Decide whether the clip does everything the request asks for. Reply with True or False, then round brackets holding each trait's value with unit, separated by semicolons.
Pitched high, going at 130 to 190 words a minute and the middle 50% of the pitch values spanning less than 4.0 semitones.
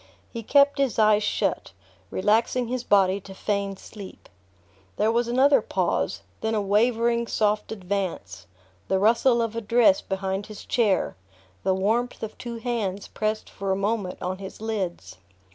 True (215 Hz; 155 wpm; 3.3 semitones)